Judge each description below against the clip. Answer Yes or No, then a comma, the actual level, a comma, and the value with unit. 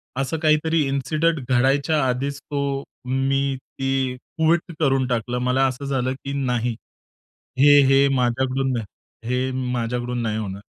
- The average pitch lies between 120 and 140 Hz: Yes, low, 135 Hz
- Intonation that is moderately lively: No, narrow, 2.1 semitones